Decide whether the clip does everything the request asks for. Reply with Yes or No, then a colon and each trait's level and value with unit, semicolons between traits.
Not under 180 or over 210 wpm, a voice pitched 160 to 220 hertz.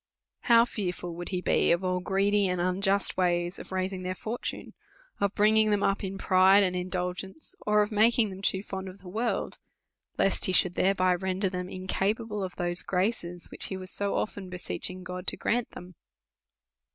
Yes: average, 190 wpm; high, 190 Hz